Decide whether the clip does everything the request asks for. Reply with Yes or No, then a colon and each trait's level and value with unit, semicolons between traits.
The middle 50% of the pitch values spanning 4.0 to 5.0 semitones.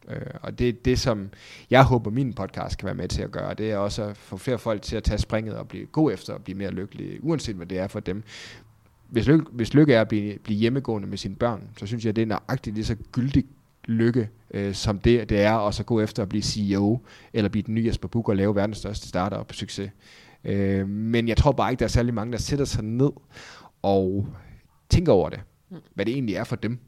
No: average, 3.0 semitones